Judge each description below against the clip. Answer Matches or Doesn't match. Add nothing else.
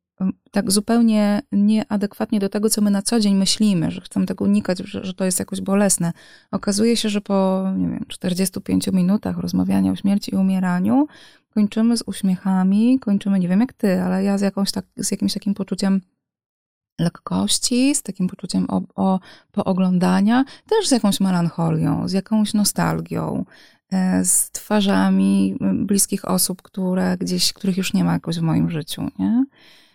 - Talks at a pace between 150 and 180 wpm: Matches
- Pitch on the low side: Doesn't match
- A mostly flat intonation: Matches